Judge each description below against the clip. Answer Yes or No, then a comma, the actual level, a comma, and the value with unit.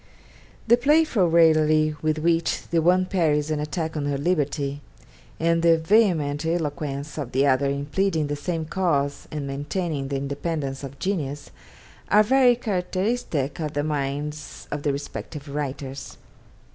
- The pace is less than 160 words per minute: Yes, average, 145 wpm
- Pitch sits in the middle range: Yes, medium, 155 Hz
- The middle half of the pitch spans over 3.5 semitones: No, average, 3.2 semitones